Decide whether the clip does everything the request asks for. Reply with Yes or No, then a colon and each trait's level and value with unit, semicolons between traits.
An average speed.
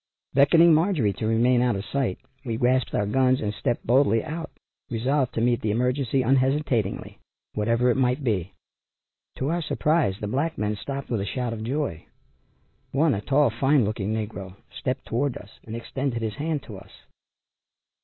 Yes: average, 175 wpm